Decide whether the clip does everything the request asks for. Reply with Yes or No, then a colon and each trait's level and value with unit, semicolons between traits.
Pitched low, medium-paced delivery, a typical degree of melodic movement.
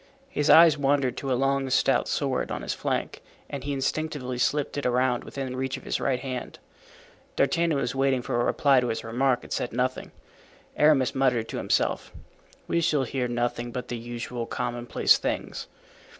No: low, 130 Hz; average, 180 wpm; narrow, 2.2 semitones